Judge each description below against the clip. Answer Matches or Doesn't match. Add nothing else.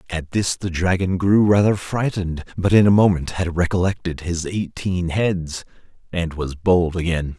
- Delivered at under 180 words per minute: Matches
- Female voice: Doesn't match